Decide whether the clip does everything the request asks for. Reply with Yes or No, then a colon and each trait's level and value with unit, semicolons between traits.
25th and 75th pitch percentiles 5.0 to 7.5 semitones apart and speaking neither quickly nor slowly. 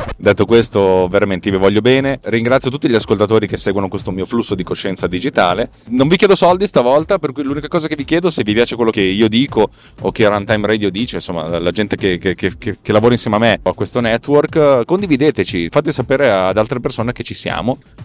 No: wide, 5.4 semitones; fast, 225 wpm